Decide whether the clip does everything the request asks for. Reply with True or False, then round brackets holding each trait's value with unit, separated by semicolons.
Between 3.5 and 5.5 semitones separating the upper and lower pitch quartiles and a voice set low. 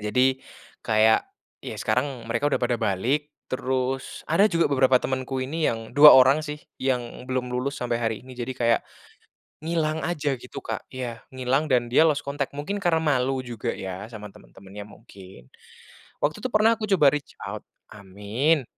True (3.9 semitones; 130 Hz)